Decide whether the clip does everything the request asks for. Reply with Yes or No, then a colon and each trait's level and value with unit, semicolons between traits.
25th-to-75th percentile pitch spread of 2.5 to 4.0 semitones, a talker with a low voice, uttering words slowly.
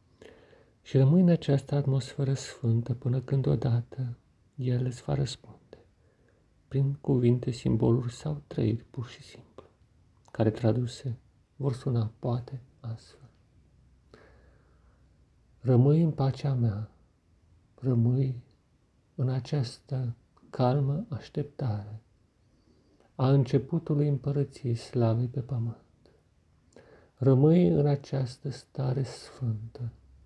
Yes: average, 3.3 semitones; low, 125 Hz; slow, 95 wpm